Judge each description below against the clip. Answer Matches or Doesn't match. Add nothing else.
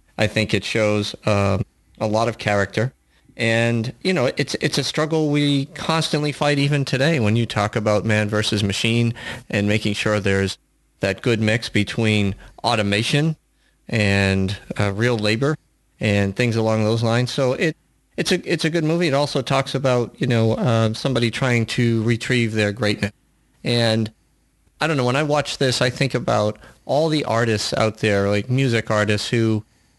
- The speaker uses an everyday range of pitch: Matches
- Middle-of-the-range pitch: Doesn't match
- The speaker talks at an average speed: Matches